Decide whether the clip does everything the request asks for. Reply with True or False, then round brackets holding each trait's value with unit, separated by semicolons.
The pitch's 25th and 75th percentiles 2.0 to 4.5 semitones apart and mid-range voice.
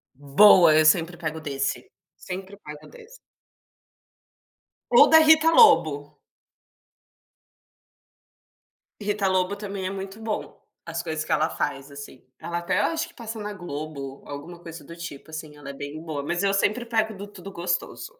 False (5.1 semitones; 175 Hz)